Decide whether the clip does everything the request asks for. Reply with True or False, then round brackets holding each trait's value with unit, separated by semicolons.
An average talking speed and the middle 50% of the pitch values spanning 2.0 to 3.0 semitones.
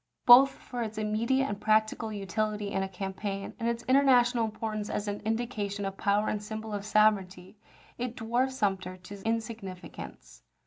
True (160 wpm; 2.5 semitones)